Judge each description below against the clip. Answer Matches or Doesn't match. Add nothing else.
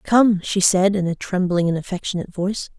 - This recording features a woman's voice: Matches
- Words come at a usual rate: Matches